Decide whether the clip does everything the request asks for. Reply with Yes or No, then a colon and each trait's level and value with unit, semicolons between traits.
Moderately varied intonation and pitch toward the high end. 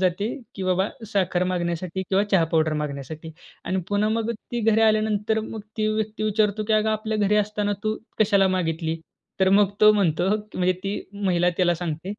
Yes: average, 3.2 semitones; high, 200 Hz